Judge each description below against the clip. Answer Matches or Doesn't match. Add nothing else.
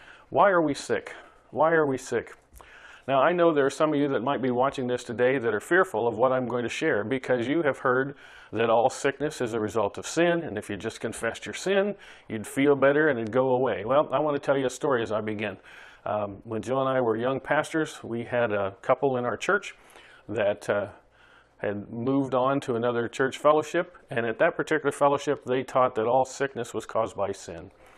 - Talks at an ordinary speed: Doesn't match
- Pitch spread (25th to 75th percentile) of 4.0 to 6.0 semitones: Doesn't match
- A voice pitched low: Matches